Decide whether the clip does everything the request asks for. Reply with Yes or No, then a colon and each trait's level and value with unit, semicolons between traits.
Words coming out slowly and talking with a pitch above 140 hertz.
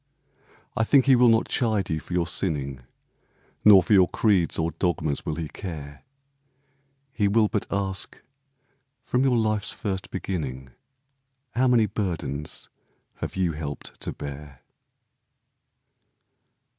No: slow, 130 wpm; very low, 95 Hz